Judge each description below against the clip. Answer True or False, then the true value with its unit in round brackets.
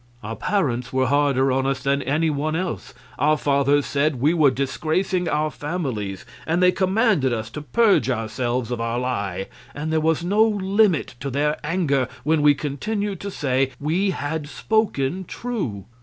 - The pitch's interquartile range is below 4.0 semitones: False (5.3 semitones)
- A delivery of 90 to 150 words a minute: False (170 wpm)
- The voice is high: False (145 Hz)